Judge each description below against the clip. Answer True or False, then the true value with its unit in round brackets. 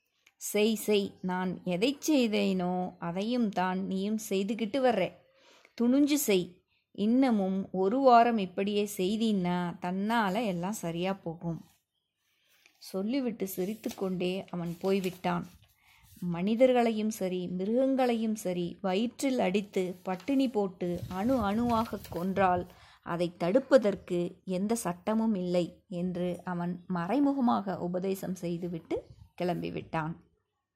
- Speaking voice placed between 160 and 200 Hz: True (190 Hz)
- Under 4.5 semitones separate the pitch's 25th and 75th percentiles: True (4.0 semitones)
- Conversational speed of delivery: True (95 wpm)